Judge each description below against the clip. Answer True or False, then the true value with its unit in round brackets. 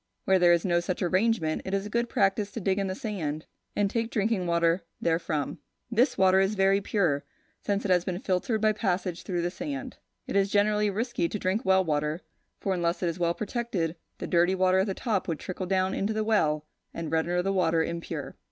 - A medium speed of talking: False (215 wpm)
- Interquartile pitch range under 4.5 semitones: True (3.2 semitones)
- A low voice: False (190 Hz)